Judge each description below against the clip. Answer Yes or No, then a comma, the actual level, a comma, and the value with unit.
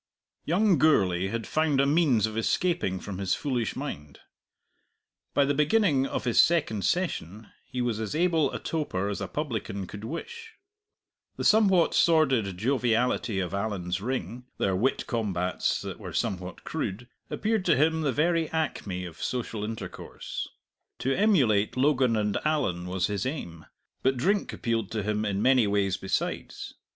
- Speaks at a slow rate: No, average, 155 wpm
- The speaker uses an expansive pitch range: Yes, wide, 7.5 semitones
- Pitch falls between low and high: No, low, 120 Hz